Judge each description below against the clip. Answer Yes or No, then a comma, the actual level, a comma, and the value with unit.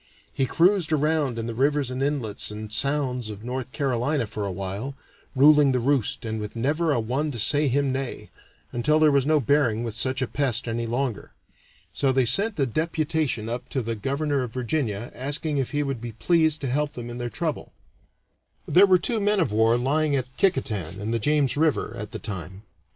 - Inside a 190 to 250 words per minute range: Yes, fast, 205 wpm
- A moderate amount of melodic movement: Yes, average, 4.4 semitones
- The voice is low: Yes, low, 130 Hz